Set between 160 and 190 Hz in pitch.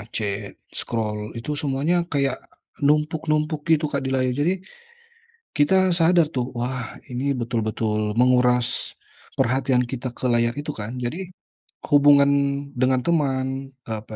No: low, 130 Hz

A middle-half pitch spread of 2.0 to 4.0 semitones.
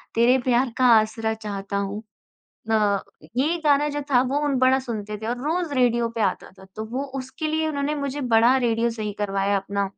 No: average, 4.7 semitones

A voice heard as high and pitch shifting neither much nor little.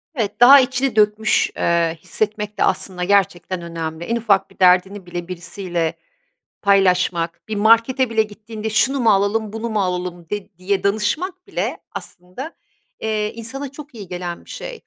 Yes: high, 205 Hz; average, 4.1 semitones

